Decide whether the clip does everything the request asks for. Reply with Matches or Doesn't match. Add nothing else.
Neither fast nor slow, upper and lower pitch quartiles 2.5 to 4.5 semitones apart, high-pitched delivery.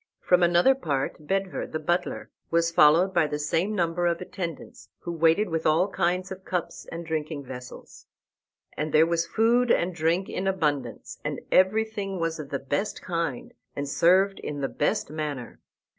Doesn't match